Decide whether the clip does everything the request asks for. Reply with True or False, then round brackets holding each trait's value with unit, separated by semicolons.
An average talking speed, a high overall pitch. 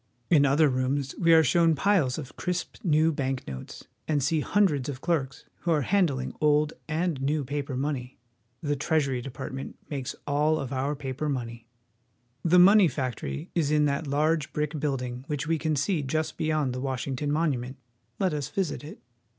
False (180 wpm; 145 Hz)